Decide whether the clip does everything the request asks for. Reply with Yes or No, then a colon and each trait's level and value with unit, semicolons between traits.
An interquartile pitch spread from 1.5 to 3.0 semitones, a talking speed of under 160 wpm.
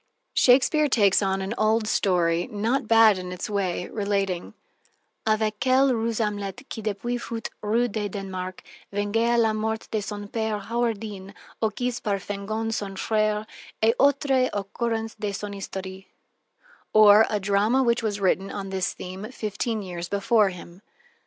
Yes: narrow, 2.5 semitones; average, 145 wpm